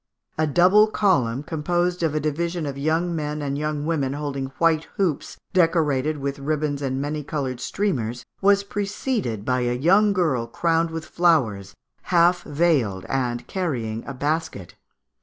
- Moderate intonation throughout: Yes, average, 4.2 semitones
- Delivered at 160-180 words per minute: No, average, 150 wpm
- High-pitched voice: No, medium, 150 Hz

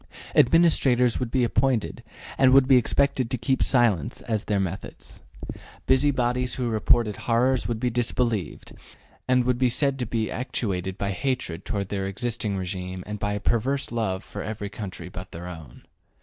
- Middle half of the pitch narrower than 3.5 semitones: No, average, 4.3 semitones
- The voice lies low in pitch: Yes, low, 115 Hz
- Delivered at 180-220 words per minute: No, average, 170 wpm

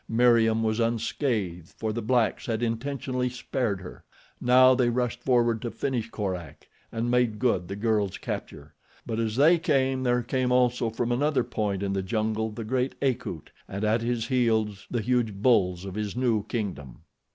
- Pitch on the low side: Yes, low, 115 Hz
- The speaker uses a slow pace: No, average, 175 wpm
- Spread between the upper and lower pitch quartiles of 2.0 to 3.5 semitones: Yes, average, 2.8 semitones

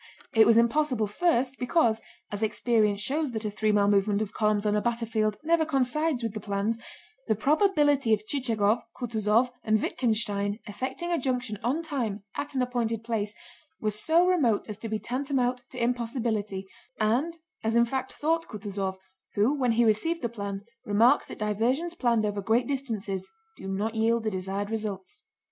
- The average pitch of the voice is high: Yes, high, 225 Hz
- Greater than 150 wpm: Yes, average, 165 wpm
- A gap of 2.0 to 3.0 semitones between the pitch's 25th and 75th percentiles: No, average, 3.7 semitones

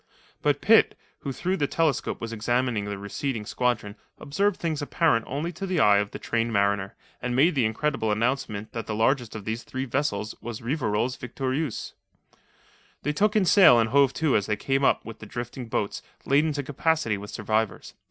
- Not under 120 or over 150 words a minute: No, average, 190 wpm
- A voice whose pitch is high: No, low, 125 Hz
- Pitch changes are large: No, average, 5.0 semitones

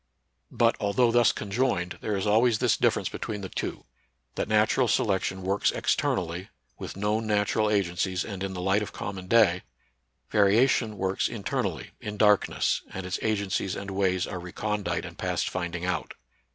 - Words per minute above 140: Yes, average, 165 wpm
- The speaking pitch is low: Yes, low, 100 Hz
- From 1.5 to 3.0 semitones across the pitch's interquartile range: Yes, narrow, 2.5 semitones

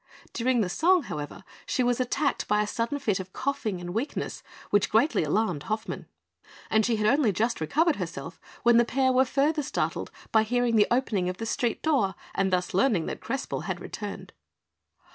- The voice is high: Yes, high, 225 Hz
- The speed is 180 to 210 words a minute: Yes, average, 185 wpm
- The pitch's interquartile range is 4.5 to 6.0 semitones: Yes, average, 5.1 semitones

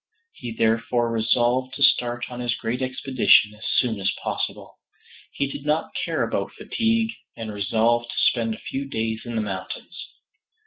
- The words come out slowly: No, average, 165 wpm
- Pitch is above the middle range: No, low, 120 Hz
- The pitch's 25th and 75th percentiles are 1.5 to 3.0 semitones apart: Yes, narrow, 2.5 semitones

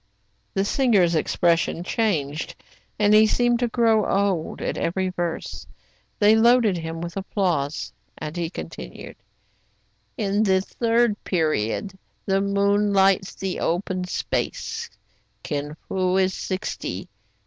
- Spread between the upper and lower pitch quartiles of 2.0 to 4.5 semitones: Yes, average, 3.6 semitones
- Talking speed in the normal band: No, slow, 120 wpm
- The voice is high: Yes, high, 195 Hz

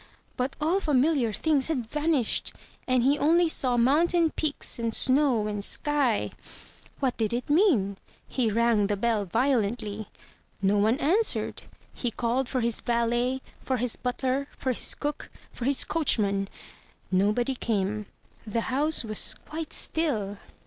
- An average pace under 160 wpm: Yes, average, 140 wpm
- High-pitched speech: Yes, very high, 250 Hz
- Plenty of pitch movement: No, average, 4.9 semitones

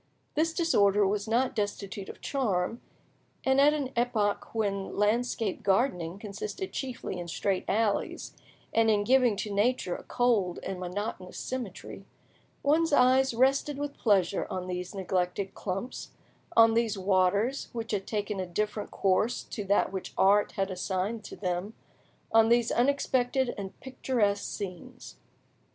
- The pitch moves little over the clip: No, average, 4.2 semitones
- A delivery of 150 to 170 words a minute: No, average, 140 wpm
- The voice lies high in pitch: Yes, high, 210 Hz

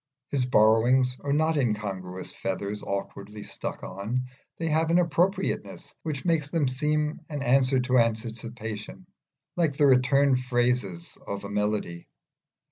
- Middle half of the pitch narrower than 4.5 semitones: No, wide, 5.6 semitones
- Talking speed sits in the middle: No, slow, 130 wpm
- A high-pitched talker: No, low, 125 Hz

